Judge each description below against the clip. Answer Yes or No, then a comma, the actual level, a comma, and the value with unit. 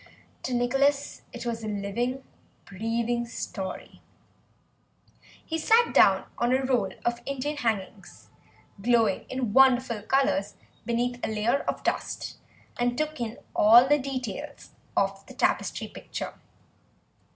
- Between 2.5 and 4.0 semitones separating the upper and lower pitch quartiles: Yes, average, 2.9 semitones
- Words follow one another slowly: Yes, slow, 125 wpm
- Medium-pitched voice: No, high, 240 Hz